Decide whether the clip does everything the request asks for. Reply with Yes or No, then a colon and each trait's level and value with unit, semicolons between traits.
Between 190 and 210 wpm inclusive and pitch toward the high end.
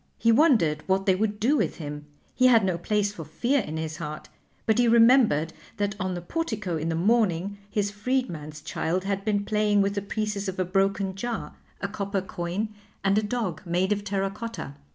Yes: average, 200 wpm; high, 200 Hz